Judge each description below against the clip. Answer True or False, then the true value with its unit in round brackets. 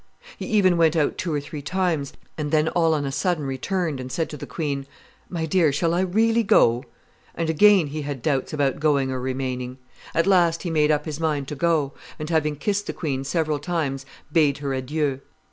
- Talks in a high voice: False (150 Hz)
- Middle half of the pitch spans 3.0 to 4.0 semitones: True (3.4 semitones)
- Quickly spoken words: True (210 wpm)